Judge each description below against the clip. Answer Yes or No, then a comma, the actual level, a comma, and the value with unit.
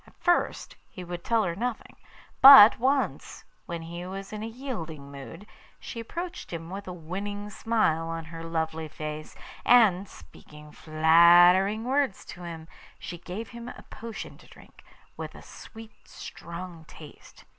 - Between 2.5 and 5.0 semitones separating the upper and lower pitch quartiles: No, wide, 5.4 semitones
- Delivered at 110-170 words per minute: Yes, average, 155 wpm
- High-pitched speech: No, medium, 180 Hz